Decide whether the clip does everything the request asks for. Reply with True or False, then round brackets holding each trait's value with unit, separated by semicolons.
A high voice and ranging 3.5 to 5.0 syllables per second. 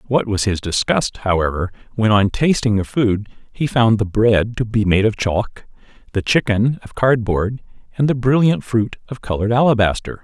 False (110 Hz; 4.9 syllables/s)